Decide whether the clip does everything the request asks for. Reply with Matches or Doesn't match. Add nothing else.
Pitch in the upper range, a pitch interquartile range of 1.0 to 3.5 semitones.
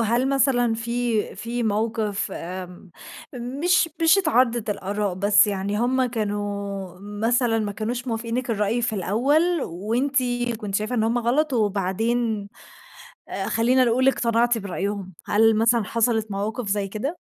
Matches